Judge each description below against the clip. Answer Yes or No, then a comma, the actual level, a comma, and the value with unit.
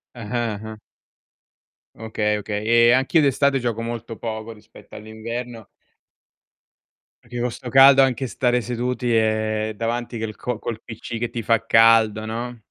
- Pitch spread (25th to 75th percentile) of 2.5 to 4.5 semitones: No, narrow, 2.0 semitones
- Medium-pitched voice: No, low, 115 Hz